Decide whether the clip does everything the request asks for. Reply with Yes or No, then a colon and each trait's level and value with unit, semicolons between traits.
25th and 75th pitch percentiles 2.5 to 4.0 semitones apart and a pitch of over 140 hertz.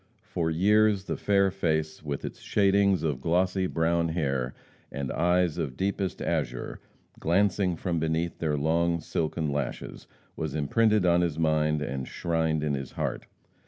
No: average, 3.1 semitones; very low, 80 Hz